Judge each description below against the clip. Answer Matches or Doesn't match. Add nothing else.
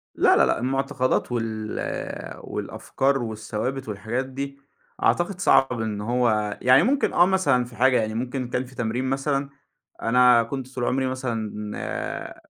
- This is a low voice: Matches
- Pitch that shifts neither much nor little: Matches